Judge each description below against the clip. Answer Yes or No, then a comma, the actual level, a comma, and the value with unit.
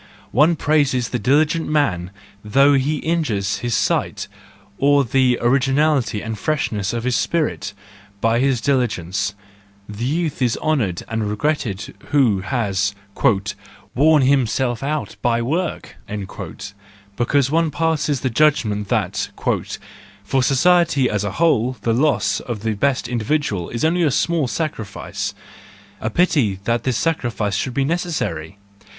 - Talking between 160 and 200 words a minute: No, slow, 135 wpm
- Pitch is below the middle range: Yes, low, 130 Hz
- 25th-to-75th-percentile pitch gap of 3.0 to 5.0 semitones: No, wide, 5.5 semitones